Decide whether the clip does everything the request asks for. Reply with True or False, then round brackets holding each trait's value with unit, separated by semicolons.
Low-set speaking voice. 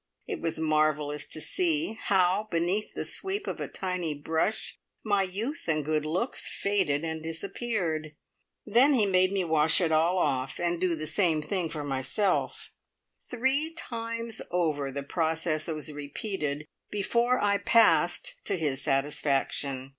False (170 Hz)